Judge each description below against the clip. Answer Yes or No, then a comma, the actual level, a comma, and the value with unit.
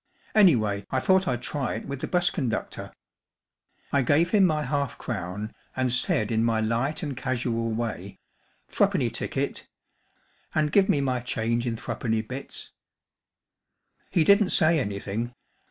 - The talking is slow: No, average, 165 wpm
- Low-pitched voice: Yes, low, 125 Hz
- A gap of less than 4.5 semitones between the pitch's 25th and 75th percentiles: No, average, 5.2 semitones